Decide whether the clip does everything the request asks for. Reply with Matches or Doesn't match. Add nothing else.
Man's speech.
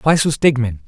Matches